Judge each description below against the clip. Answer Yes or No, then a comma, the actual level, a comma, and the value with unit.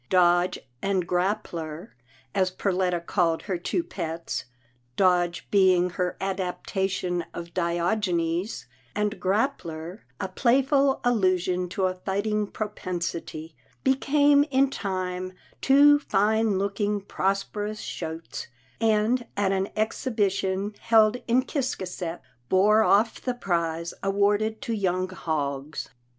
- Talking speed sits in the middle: No, slow, 115 wpm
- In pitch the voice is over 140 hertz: Yes, high, 190 Hz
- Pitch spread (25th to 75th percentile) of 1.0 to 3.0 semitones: No, average, 3.4 semitones